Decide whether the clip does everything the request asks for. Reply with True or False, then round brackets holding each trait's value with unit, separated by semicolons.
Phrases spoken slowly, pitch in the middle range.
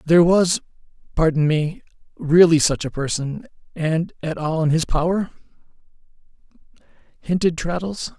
True (105 wpm; 165 Hz)